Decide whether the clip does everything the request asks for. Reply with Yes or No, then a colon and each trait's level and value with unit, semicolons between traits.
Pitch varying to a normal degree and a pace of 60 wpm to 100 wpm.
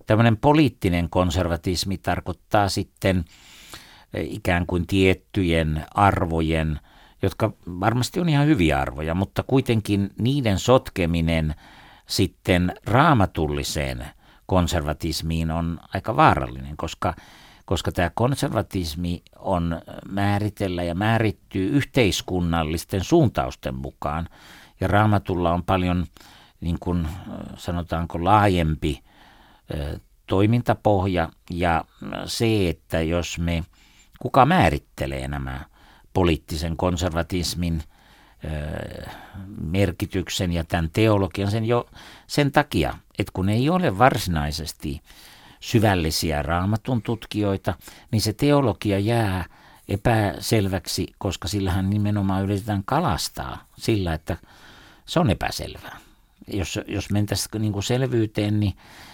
Yes: average, 4.0 semitones; slow, 95 wpm